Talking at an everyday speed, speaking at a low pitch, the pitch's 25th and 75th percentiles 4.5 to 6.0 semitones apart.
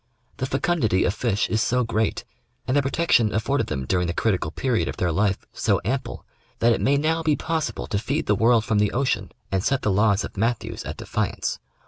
No: fast, 210 wpm; low, 115 Hz; average, 5.0 semitones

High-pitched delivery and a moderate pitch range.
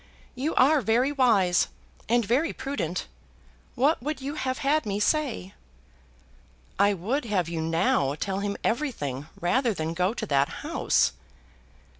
No: high, 220 Hz; wide, 7.2 semitones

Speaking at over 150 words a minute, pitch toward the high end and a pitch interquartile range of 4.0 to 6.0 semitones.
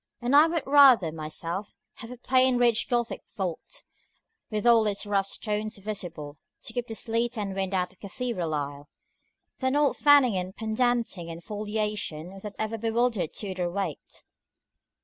Yes: average, 165 wpm; high, 215 Hz; average, 4.6 semitones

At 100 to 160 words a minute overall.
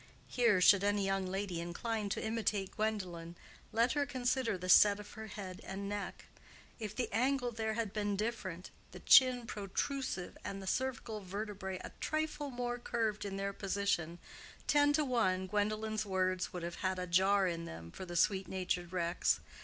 No: average, 175 wpm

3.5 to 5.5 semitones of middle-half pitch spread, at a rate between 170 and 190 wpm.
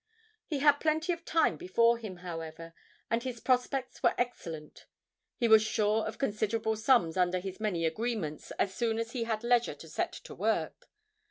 Yes: average, 4.9 semitones; average, 175 wpm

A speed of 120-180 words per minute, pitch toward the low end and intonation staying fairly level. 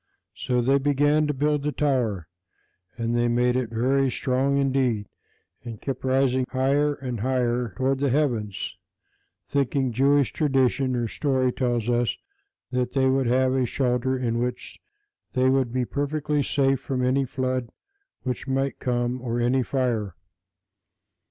Yes: average, 150 wpm; low, 130 Hz; narrow, 2.0 semitones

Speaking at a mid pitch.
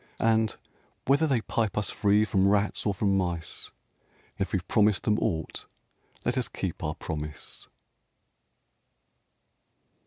No: low, 105 Hz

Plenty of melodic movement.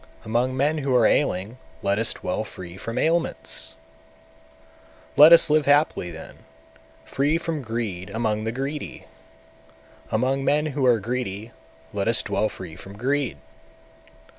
Yes: wide, 5.9 semitones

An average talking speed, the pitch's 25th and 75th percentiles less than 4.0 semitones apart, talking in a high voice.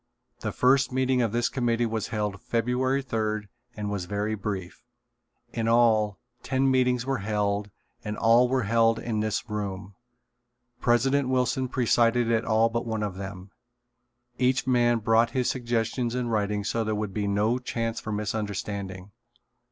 No: average, 155 wpm; average, 2.8 semitones; low, 115 Hz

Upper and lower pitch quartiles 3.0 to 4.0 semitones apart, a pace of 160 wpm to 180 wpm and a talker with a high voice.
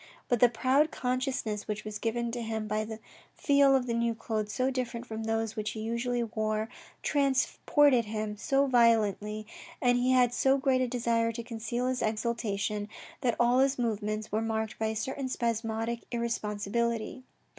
No: narrow, 2.6 semitones; average, 165 wpm; high, 230 Hz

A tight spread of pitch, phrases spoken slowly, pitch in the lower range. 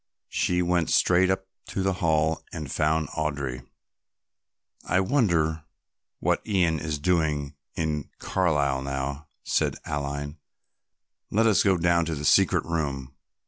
No: average, 3.6 semitones; slow, 130 wpm; very low, 80 Hz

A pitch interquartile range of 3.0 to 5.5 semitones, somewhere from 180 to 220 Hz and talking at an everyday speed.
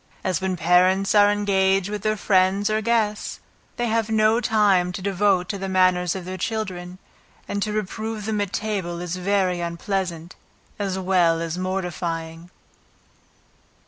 No: narrow, 2.6 semitones; high, 190 Hz; average, 150 wpm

